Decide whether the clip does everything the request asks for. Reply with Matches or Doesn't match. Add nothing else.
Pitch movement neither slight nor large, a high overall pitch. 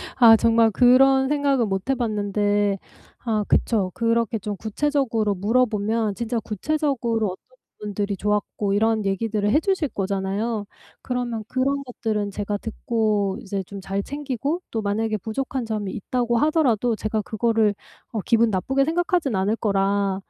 Matches